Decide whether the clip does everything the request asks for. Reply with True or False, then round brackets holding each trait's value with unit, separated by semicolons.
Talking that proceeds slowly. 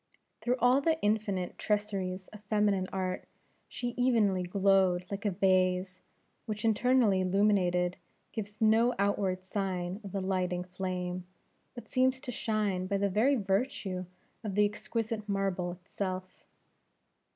True (130 wpm)